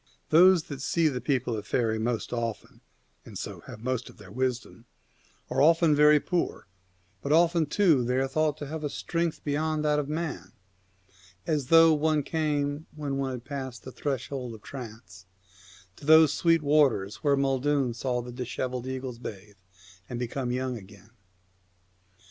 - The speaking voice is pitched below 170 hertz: Yes, low, 135 Hz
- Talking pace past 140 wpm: Yes, average, 165 wpm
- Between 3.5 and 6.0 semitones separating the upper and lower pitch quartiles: Yes, average, 3.8 semitones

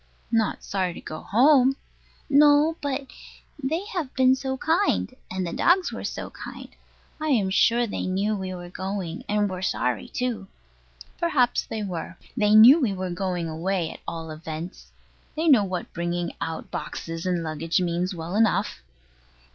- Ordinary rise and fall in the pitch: No, wide, 6.9 semitones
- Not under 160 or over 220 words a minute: Yes, average, 165 wpm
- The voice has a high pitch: Yes, high, 195 Hz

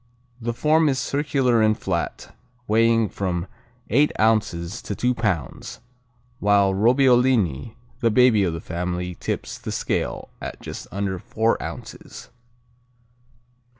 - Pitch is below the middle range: Yes, low, 110 Hz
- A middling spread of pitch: Yes, average, 4.6 semitones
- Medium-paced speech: No, slow, 120 wpm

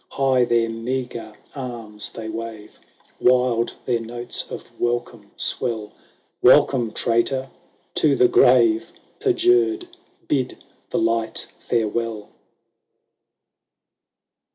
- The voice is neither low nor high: No, low, 120 Hz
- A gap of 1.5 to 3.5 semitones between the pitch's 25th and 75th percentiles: Yes, average, 2.7 semitones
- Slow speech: Yes, slow, 95 wpm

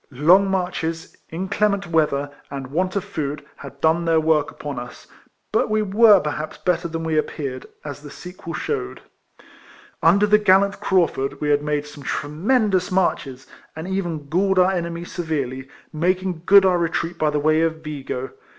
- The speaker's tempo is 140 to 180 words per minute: Yes, average, 165 wpm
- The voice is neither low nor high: Yes, medium, 165 Hz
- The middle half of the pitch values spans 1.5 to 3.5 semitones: No, average, 4.1 semitones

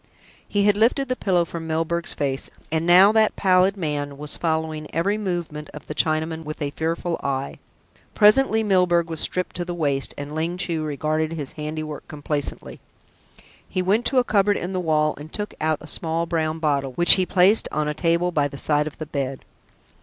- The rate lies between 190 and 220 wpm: Yes, average, 195 wpm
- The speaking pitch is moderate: Yes, medium, 160 Hz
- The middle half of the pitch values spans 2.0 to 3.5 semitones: Yes, average, 3.1 semitones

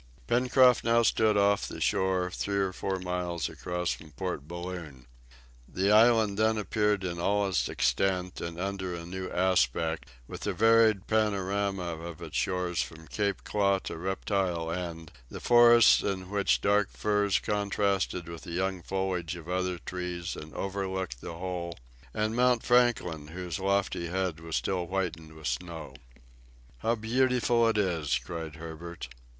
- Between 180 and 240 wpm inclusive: No, average, 155 wpm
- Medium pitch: No, very low, 95 Hz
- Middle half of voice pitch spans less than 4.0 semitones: Yes, average, 3.0 semitones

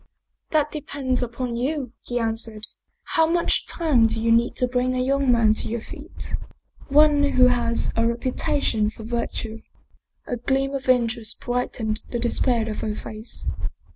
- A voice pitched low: No, high, 245 Hz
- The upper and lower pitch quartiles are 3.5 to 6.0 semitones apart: No, average, 2.9 semitones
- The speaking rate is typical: Yes, average, 170 wpm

